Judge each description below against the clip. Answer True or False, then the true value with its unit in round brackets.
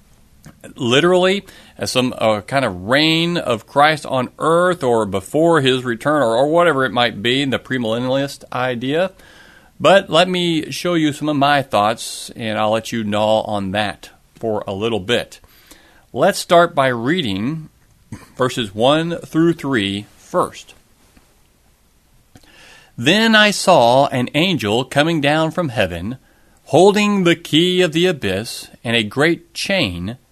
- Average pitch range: False (6.5 semitones)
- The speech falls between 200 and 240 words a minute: False (145 wpm)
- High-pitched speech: False (140 Hz)